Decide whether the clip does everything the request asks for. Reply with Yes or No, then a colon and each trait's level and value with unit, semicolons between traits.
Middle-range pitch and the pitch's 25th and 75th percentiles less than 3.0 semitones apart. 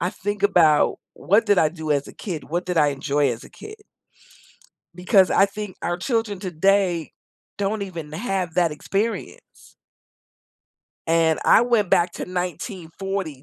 No: medium, 180 Hz; average, 3.7 semitones